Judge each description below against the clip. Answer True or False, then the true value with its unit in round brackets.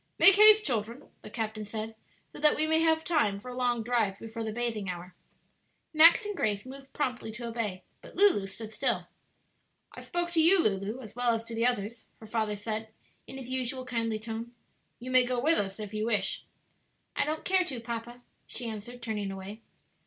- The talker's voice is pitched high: True (235 Hz)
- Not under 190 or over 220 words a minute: True (200 wpm)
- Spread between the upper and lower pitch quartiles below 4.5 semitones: True (3.4 semitones)